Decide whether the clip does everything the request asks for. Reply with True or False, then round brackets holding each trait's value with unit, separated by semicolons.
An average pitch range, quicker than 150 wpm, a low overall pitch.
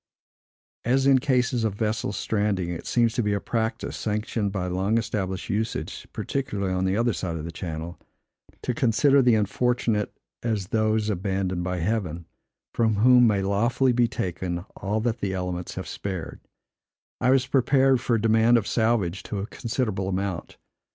True (4.0 semitones; 165 wpm; 110 Hz)